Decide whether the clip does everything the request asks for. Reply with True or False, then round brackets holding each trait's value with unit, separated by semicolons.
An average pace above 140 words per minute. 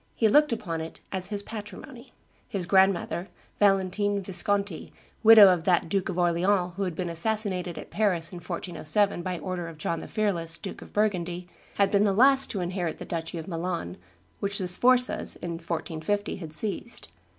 True (175 wpm)